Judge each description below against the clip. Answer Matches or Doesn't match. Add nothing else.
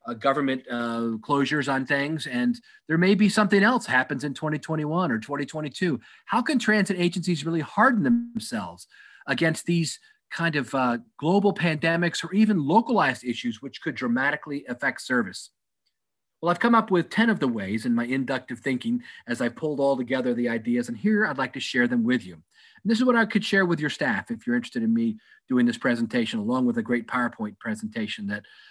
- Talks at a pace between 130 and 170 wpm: Doesn't match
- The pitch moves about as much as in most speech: Doesn't match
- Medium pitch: Matches